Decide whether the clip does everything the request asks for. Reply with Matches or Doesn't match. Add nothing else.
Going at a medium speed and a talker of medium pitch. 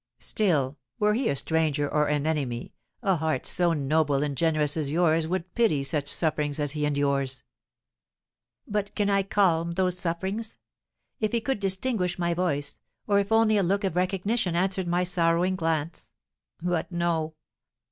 Matches